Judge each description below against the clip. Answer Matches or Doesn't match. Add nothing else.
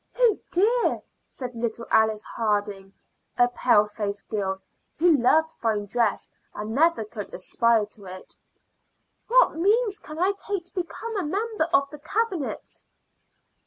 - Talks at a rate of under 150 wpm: Matches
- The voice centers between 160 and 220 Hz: Doesn't match